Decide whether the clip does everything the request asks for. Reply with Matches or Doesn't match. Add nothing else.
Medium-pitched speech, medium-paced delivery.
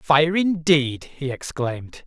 Doesn't match